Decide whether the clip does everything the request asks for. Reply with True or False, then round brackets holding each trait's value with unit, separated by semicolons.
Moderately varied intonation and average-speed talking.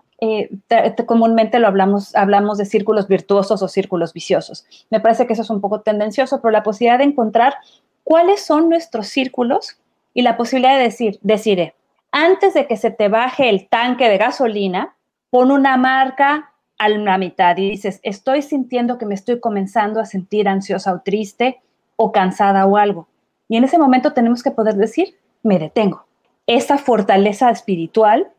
True (4.0 semitones; 175 wpm)